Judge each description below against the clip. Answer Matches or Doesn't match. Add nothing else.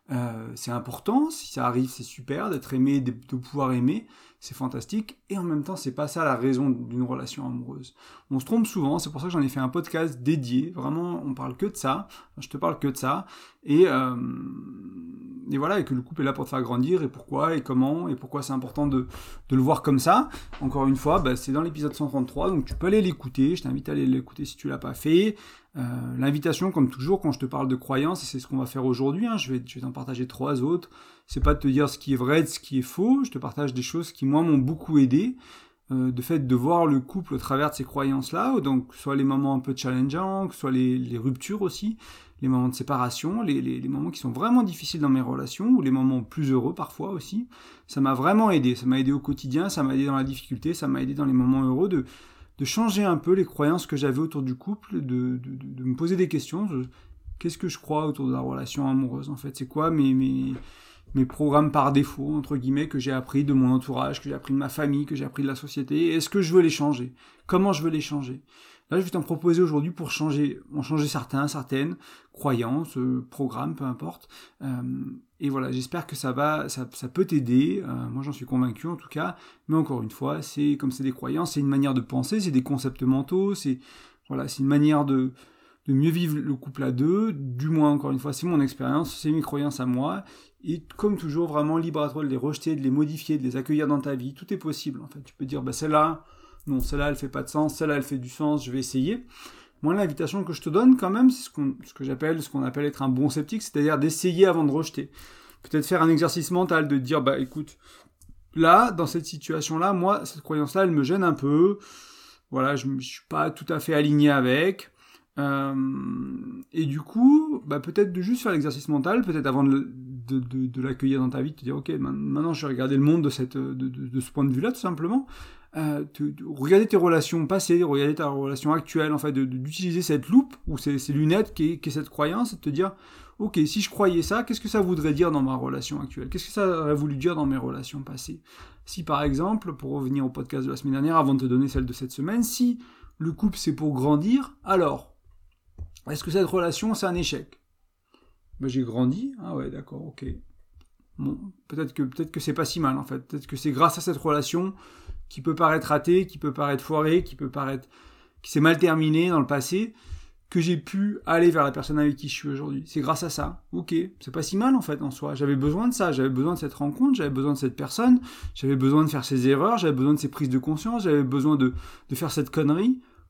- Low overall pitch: Doesn't match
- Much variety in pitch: Doesn't match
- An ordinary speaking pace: Doesn't match